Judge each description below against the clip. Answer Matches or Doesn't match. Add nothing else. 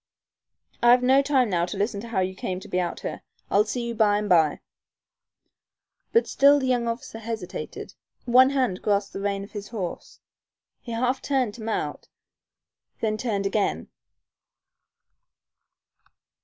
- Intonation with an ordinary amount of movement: Matches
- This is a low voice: Doesn't match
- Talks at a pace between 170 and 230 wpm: Doesn't match